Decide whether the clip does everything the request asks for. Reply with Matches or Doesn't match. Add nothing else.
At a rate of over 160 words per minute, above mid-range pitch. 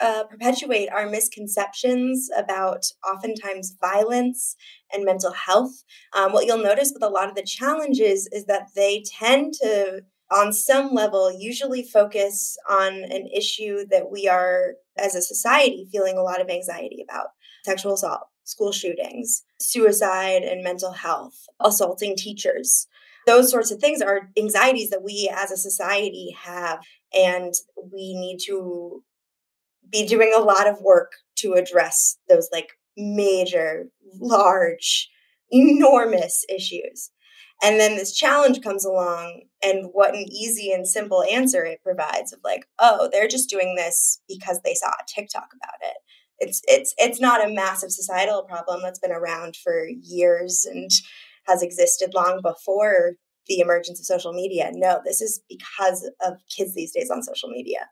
Doesn't match